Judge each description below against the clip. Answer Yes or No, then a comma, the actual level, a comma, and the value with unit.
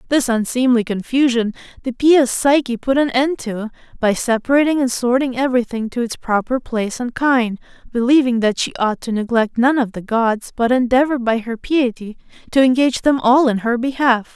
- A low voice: No, high, 245 Hz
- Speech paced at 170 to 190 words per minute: Yes, average, 180 wpm